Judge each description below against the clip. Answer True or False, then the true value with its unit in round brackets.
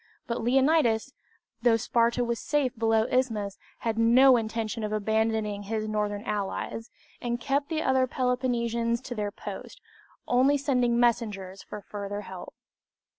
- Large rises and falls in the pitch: False (2.7 semitones)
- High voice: True (230 Hz)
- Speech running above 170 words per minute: False (140 wpm)